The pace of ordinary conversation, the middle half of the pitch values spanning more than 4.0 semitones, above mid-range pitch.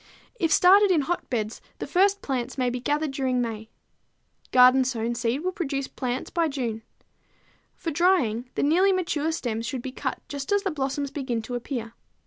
Yes: average, 175 wpm; average, 5.1 semitones; very high, 270 Hz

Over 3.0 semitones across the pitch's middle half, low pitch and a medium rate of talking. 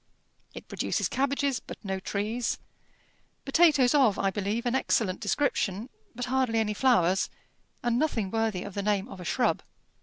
No: average, 4.6 semitones; high, 225 Hz; average, 155 wpm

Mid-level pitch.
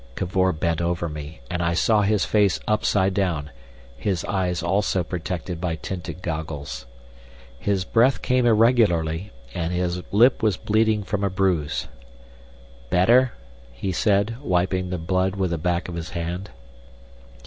No: very low, 90 Hz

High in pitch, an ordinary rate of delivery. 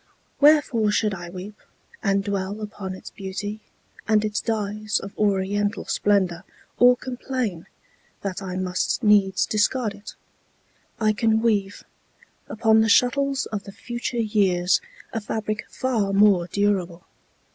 No: high, 210 Hz; slow, 130 wpm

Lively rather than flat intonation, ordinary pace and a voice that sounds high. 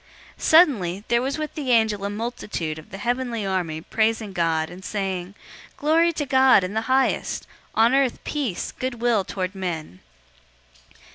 Yes: wide, 5.8 semitones; average, 165 wpm; high, 220 Hz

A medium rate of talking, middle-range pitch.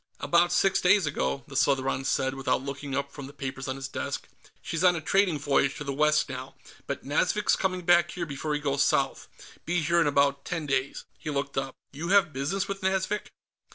No: fast, 210 wpm; medium, 145 Hz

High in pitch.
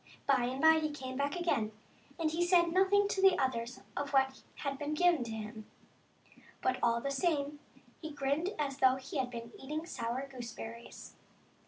Yes: very high, 275 Hz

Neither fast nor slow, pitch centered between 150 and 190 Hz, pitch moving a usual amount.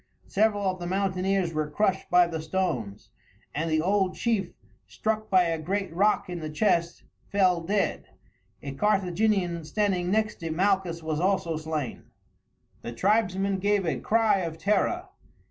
Yes: average, 150 wpm; medium, 185 Hz; average, 3.5 semitones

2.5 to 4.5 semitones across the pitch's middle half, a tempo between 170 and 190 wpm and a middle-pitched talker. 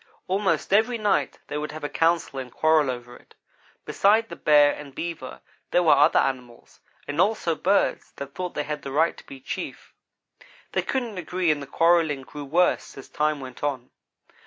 Yes: average, 4.2 semitones; average, 185 wpm; medium, 150 Hz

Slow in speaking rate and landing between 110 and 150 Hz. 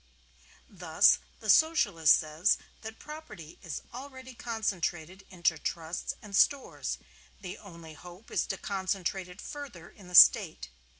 No: slow, 130 wpm; high, 190 Hz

